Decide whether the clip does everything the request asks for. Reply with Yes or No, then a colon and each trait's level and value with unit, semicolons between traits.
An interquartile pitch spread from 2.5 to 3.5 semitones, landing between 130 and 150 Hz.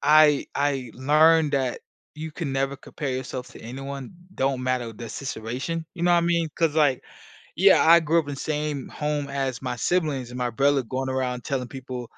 Yes: average, 3.0 semitones; low, 135 Hz